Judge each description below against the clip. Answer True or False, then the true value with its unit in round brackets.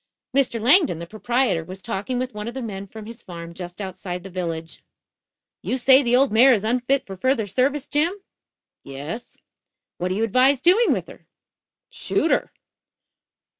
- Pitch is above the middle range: True (225 Hz)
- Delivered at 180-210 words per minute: False (170 wpm)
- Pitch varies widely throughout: True (5.9 semitones)